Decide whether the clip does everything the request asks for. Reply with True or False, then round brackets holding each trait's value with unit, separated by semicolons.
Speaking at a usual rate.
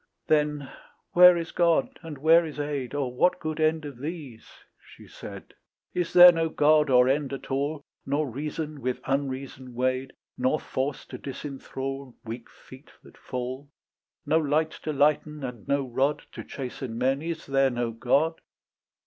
True (160 wpm)